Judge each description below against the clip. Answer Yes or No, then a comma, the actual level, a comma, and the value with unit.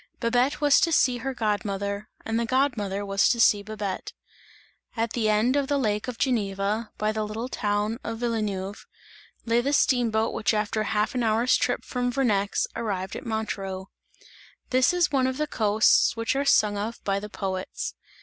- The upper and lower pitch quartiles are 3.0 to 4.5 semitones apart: Yes, average, 3.3 semitones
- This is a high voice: Yes, high, 220 Hz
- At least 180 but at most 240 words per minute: Yes, average, 190 wpm